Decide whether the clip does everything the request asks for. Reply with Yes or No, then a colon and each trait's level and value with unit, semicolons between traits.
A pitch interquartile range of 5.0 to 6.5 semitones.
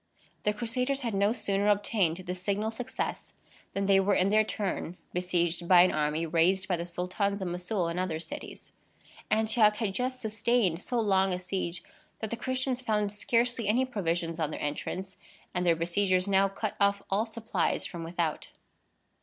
No: average, 3.6 semitones